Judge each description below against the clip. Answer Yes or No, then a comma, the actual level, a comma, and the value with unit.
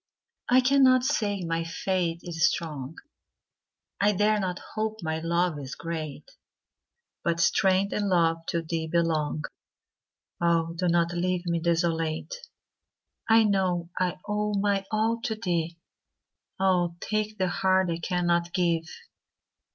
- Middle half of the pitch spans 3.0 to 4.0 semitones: Yes, average, 3.4 semitones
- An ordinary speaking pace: No, slow, 115 wpm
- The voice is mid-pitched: Yes, medium, 175 Hz